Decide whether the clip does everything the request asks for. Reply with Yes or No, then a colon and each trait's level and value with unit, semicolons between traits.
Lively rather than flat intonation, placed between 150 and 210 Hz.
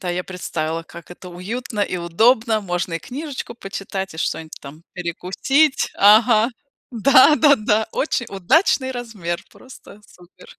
Yes: wide, 5.8 semitones; high, 205 Hz